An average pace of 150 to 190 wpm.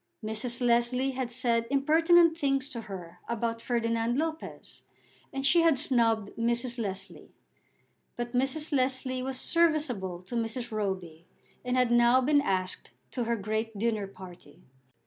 No: average, 140 wpm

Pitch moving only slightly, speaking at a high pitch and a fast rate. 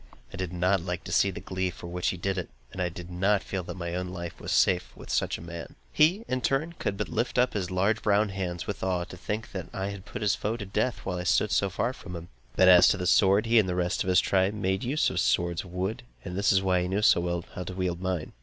No: narrow, 2.2 semitones; very low, 95 Hz; fast, 295 wpm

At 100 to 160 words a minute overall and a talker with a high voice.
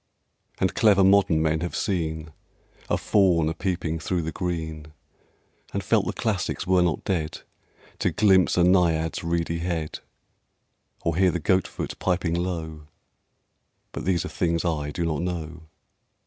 No: average, 150 wpm; very low, 85 Hz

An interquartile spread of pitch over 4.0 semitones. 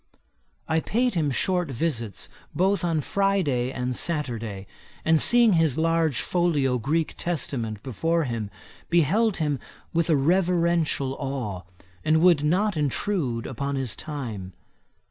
Yes: average, 5.2 semitones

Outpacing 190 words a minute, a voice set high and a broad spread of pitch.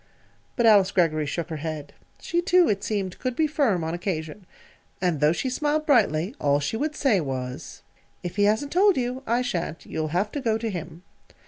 Yes: average, 200 wpm; high, 195 Hz; wide, 8.0 semitones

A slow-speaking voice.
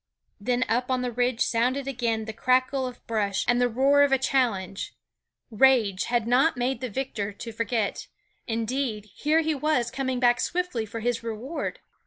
No: average, 175 wpm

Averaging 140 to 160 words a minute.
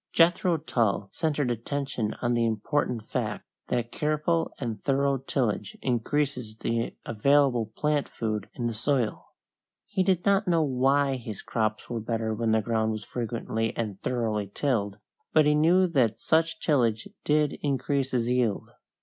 Yes: average, 150 wpm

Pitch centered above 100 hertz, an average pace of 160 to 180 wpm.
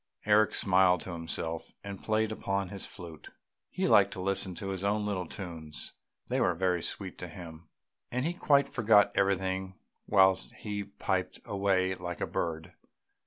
No: very low, 95 Hz; average, 165 wpm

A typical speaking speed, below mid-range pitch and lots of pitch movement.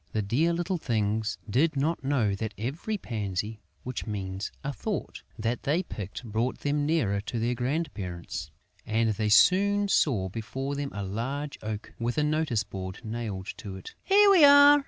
Yes: average, 170 wpm; low, 120 Hz; wide, 6.4 semitones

